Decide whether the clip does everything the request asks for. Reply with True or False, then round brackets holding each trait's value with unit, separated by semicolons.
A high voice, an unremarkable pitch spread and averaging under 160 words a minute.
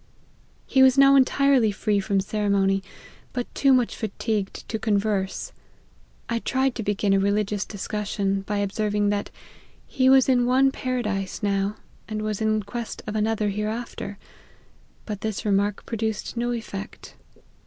True (215 Hz; 3.0 semitones; 150 wpm)